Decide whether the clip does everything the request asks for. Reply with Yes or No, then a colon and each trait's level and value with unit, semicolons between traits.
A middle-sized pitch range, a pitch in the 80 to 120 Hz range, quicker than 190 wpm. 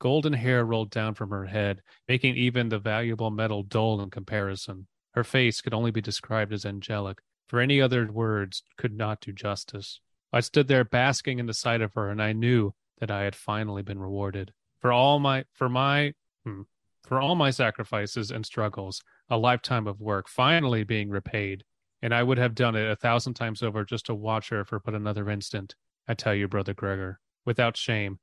Yes: average, 3.1 semitones; low, 110 Hz; average, 200 wpm